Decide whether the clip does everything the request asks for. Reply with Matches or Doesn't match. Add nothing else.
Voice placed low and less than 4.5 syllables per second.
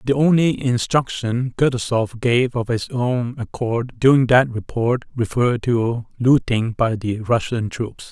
Matches